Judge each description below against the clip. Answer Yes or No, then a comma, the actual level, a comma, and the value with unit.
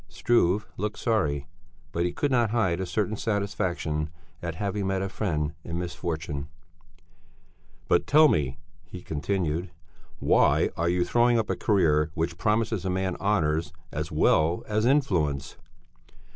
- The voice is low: Yes, very low, 90 Hz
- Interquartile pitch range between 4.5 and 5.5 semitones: Yes, average, 5.0 semitones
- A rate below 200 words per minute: Yes, average, 145 wpm